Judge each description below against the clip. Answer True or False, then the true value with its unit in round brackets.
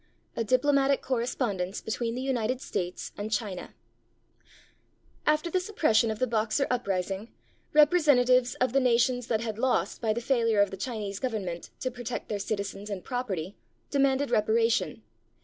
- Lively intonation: False (3.7 semitones)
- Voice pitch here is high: True (235 Hz)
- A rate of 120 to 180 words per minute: True (150 wpm)